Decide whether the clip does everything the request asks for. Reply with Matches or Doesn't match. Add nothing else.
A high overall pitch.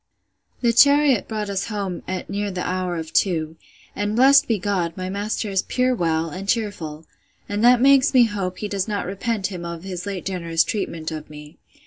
Matches